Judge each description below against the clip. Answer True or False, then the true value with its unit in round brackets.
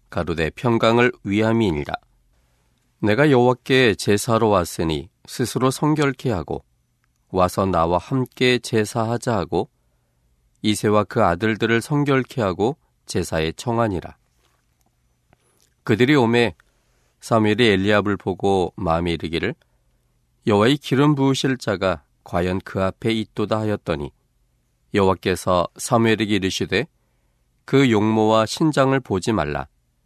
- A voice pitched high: False (105 Hz)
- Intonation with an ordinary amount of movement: False (6.1 semitones)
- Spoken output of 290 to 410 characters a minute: False (260 characters per minute)